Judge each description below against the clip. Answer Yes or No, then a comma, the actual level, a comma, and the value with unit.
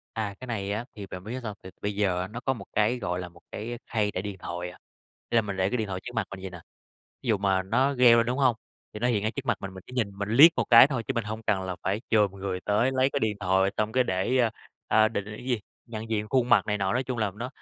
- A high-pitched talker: No, low, 105 Hz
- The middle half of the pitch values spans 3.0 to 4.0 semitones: Yes, average, 3.6 semitones